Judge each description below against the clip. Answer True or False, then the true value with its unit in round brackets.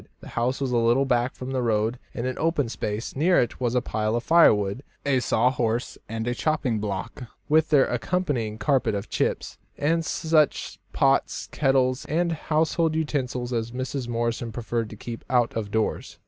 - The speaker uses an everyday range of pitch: True (3.8 semitones)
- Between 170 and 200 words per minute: True (175 wpm)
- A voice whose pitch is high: False (125 Hz)